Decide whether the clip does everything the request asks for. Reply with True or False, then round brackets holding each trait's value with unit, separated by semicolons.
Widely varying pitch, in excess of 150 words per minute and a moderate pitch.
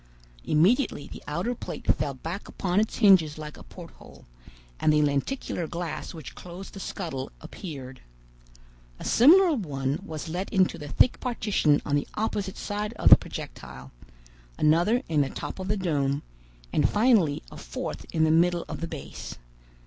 True (5.7 semitones; 165 wpm; 170 Hz)